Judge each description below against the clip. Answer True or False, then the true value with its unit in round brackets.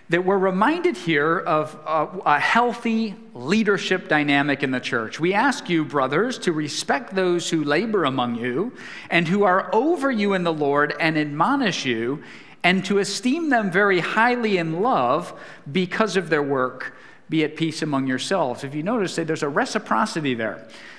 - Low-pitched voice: False (170 Hz)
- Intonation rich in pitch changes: True (6.3 semitones)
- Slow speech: False (165 wpm)